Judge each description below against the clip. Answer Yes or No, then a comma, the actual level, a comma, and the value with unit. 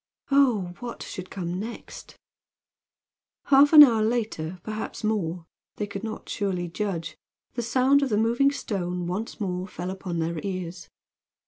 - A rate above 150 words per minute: No, average, 145 wpm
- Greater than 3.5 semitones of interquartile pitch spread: Yes, average, 4.6 semitones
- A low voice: No, high, 200 Hz